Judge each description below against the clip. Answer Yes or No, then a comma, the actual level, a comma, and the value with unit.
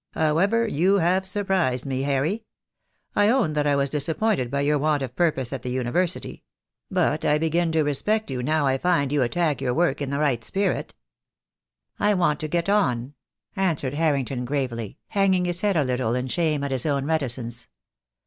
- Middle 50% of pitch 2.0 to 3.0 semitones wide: No, average, 5.0 semitones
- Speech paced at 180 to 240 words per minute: Yes, average, 190 wpm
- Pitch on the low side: No, medium, 150 Hz